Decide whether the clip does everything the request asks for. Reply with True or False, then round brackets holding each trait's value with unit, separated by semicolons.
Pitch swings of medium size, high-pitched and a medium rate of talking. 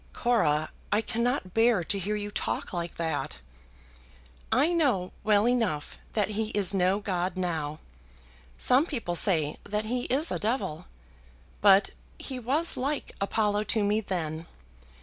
True (5.0 semitones; 205 Hz; 145 wpm)